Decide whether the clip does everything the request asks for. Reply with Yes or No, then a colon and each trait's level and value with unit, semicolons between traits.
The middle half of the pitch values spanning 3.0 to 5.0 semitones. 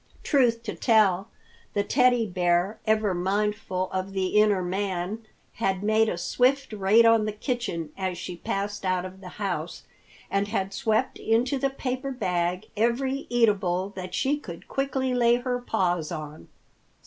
Yes: average, 4.3 semitones